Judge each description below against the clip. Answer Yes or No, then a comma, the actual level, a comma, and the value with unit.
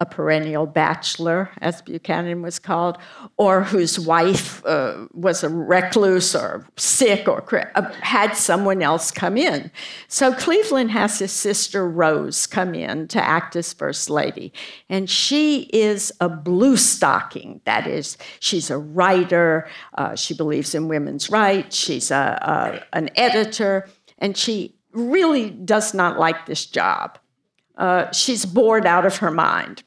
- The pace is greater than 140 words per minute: Yes, average, 150 wpm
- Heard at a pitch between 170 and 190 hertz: Yes, medium, 185 Hz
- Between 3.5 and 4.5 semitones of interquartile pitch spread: Yes, average, 4.1 semitones